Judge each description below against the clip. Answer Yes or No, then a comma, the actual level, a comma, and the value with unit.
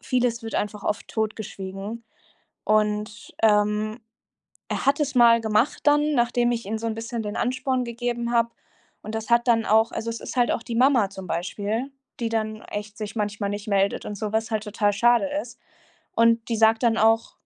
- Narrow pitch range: Yes, narrow, 2.1 semitones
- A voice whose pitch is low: No, high, 225 Hz